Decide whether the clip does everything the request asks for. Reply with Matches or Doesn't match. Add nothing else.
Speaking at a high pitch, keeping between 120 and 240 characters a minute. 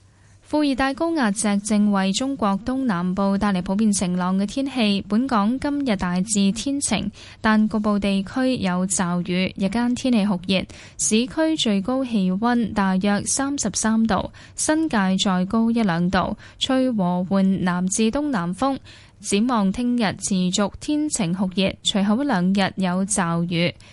Matches